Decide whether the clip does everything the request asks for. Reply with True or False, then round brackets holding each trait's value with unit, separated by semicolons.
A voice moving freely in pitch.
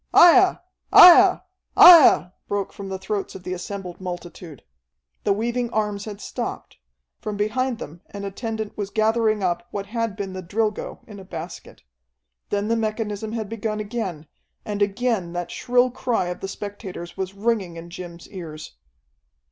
False (3.3 semitones)